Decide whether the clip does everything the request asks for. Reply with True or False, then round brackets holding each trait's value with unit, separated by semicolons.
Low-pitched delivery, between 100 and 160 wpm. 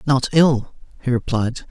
True (130 Hz; 140 wpm)